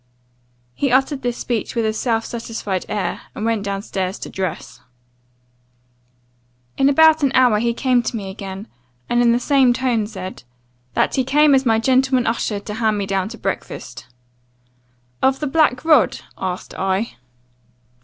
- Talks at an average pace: Yes, average, 165 wpm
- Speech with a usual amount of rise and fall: Yes, average, 4.5 semitones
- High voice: Yes, high, 230 Hz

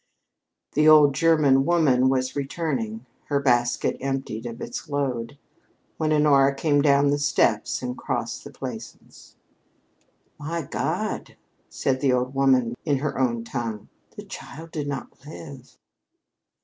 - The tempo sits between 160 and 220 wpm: No, slow, 135 wpm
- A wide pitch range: No, average, 2.7 semitones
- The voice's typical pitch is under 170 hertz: Yes, low, 135 Hz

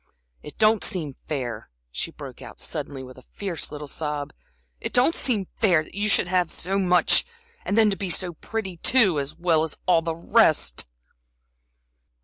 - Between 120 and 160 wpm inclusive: No, average, 175 wpm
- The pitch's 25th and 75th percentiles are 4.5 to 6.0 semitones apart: Yes, average, 4.9 semitones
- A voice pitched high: No, medium, 175 Hz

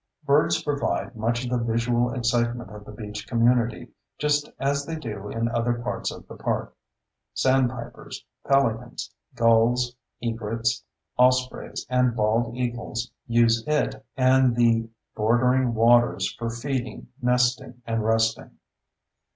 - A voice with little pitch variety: Yes, narrow, 1.7 semitones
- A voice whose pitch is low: Yes, low, 120 Hz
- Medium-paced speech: No, slow, 125 wpm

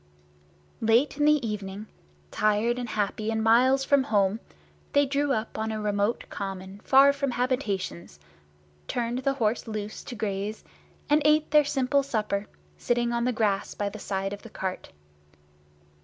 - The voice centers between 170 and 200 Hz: No, high, 225 Hz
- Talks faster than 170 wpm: No, average, 155 wpm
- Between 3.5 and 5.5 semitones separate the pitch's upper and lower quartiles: Yes, average, 4.4 semitones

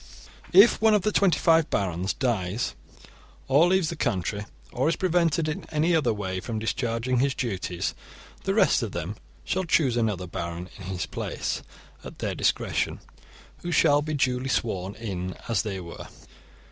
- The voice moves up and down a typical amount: No, wide, 8.9 semitones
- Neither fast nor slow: Yes, average, 170 wpm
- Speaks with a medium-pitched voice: No, low, 120 Hz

